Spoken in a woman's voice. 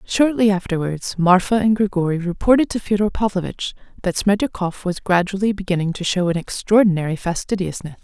Yes: female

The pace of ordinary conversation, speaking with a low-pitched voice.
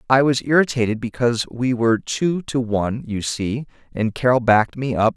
Yes: average, 185 wpm; low, 120 Hz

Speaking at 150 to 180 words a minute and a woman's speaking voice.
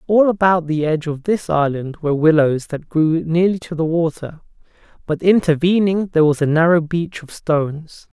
No: average, 175 wpm; male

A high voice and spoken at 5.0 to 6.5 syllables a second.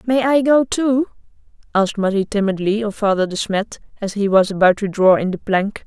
Yes: high, 210 Hz; 5.4 syllables/s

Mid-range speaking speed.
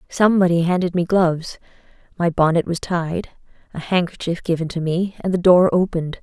Yes: average, 165 wpm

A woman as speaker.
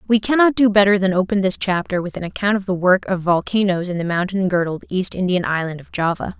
Yes: female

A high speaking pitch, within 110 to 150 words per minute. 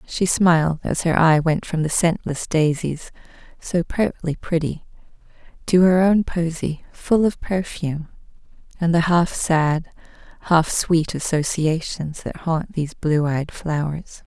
No: medium, 165 Hz; average, 140 wpm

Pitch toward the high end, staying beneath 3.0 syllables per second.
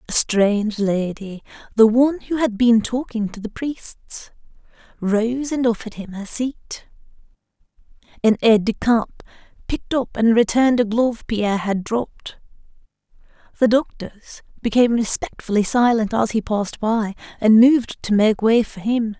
No: high, 225 Hz; 4.8 syllables/s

